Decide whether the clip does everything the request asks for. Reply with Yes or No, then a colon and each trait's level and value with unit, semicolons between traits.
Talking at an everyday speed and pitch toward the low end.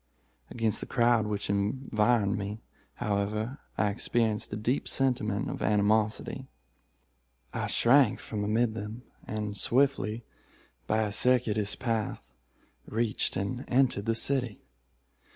No: slow, 115 wpm; low, 110 Hz